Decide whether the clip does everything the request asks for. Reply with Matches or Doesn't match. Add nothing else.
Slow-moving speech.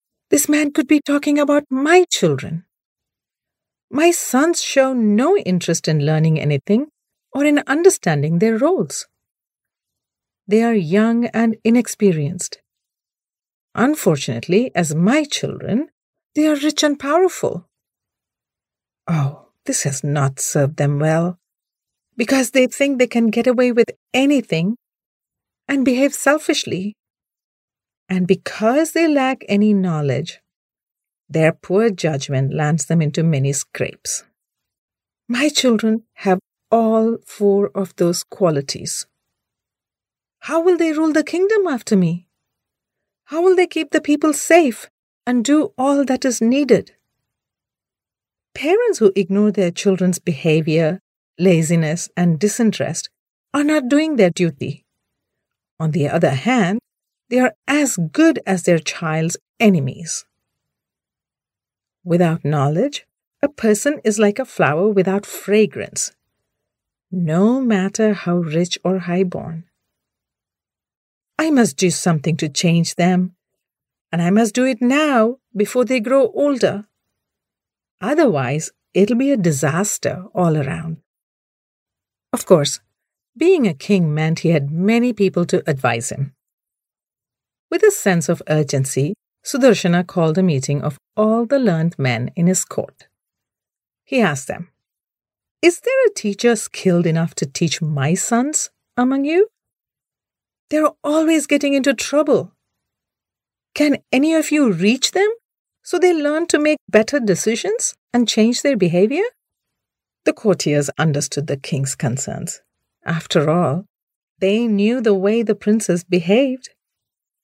Matches